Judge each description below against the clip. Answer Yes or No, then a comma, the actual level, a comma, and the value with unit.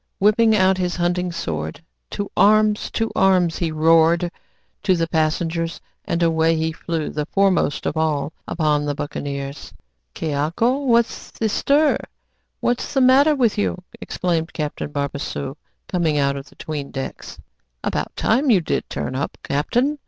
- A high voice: No, medium, 170 Hz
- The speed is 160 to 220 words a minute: No, average, 150 wpm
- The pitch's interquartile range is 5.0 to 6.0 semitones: Yes, wide, 5.6 semitones